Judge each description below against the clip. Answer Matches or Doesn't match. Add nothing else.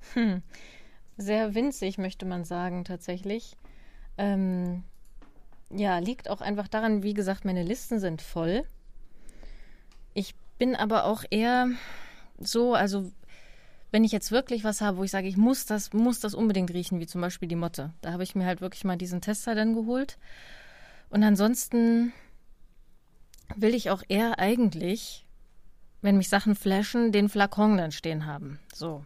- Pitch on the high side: Matches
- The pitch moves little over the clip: Doesn't match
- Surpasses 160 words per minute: Doesn't match